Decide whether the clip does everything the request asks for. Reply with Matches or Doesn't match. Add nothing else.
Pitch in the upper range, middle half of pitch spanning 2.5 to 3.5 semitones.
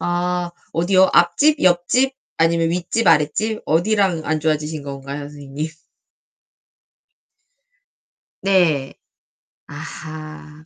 Doesn't match